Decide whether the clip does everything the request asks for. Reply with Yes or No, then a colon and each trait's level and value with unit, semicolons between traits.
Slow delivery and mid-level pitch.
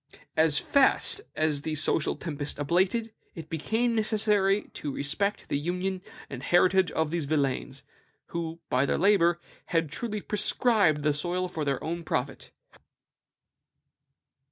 Yes: slow, 130 wpm; medium, 170 Hz